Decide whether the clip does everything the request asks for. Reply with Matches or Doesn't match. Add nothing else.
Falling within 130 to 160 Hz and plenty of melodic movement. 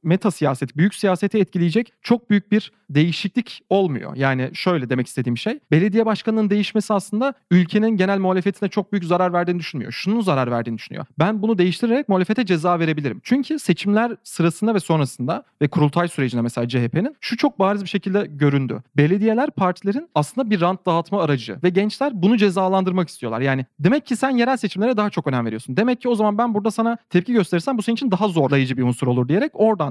Doesn't match